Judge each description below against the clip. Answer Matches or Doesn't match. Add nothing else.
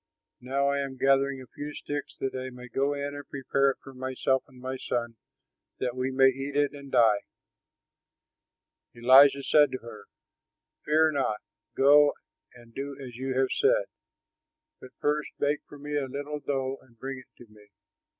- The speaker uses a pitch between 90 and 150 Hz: Matches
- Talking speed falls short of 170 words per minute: Doesn't match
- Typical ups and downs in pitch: Doesn't match